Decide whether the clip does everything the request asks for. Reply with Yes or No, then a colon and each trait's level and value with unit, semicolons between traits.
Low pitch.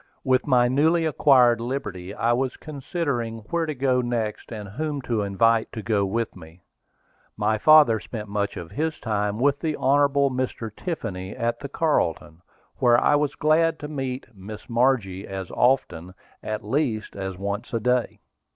Yes: low, 120 Hz